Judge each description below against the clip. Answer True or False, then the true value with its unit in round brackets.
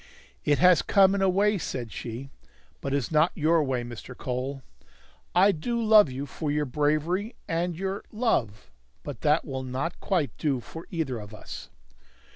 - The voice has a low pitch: False (150 Hz)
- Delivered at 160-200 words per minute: True (175 wpm)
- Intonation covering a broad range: True (5.7 semitones)